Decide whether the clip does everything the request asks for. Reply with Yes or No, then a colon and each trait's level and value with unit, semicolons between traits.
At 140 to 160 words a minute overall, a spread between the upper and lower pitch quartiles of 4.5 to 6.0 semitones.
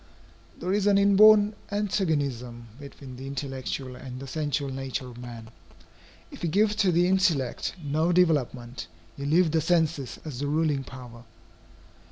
Yes: average, 150 wpm; wide, 5.5 semitones